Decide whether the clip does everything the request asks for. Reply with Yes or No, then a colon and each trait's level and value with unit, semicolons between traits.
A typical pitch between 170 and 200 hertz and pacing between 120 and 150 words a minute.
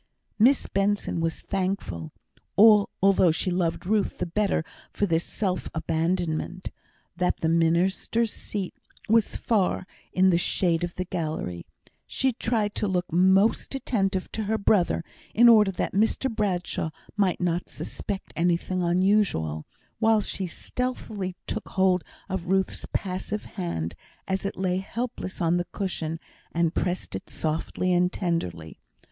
Yes: medium, 185 Hz; average, 140 wpm